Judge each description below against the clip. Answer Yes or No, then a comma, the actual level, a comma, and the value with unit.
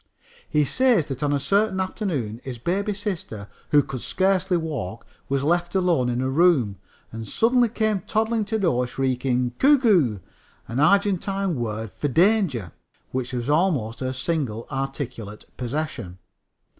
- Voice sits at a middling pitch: Yes, medium, 150 Hz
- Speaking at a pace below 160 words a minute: Yes, average, 150 wpm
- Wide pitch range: Yes, wide, 7.8 semitones